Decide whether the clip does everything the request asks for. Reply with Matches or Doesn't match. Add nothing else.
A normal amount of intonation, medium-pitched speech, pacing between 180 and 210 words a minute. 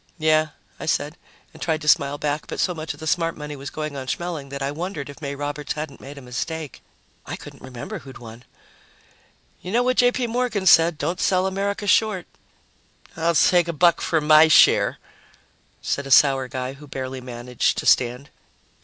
Matches